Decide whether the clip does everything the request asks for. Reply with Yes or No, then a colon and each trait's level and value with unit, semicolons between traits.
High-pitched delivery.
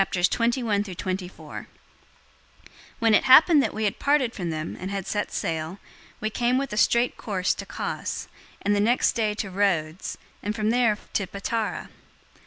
Yes: high, 210 Hz